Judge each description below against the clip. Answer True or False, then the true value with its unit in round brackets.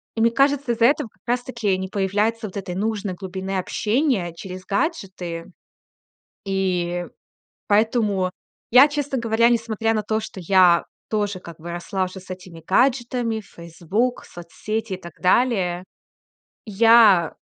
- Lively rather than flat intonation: False (4.0 semitones)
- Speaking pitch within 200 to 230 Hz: True (205 Hz)